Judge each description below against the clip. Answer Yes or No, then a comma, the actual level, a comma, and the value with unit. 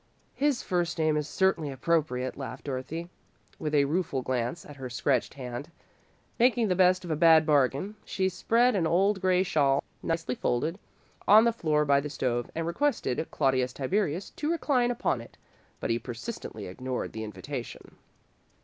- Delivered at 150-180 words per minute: Yes, average, 165 wpm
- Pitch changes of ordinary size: No, wide, 6.3 semitones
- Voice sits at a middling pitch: Yes, medium, 155 Hz